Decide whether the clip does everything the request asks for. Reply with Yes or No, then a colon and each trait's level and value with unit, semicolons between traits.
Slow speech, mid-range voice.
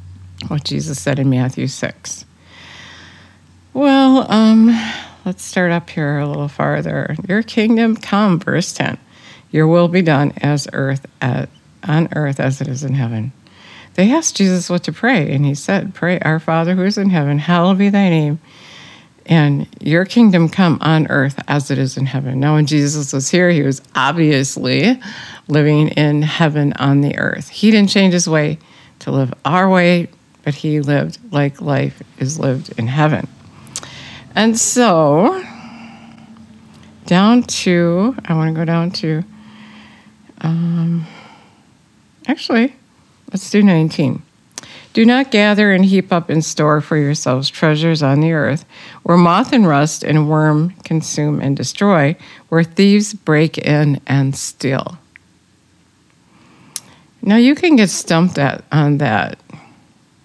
No: average, 150 wpm; medium, 155 Hz